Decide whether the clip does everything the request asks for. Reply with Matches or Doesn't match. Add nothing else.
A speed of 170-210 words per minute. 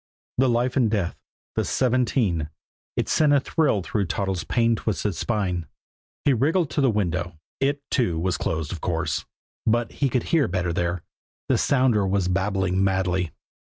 Doesn't match